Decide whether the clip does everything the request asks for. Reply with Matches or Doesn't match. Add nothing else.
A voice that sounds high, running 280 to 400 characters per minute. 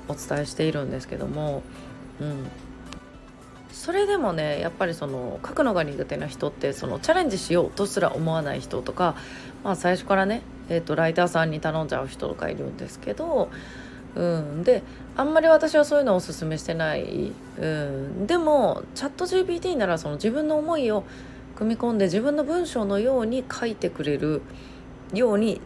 Doesn't match